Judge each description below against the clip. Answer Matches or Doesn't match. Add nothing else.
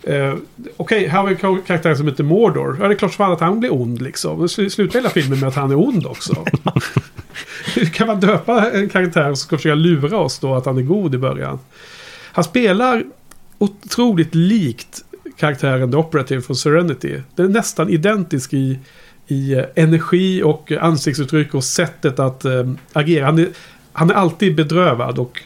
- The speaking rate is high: Doesn't match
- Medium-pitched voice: Matches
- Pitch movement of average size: Doesn't match